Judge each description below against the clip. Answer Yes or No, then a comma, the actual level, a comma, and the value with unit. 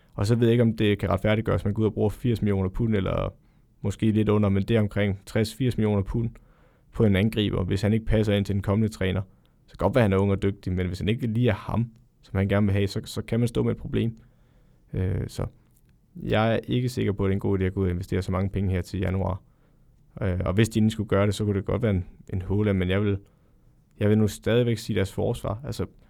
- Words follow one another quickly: Yes, fast, 275 wpm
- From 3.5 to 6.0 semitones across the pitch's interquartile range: No, average, 2.9 semitones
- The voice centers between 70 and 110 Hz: Yes, low, 105 Hz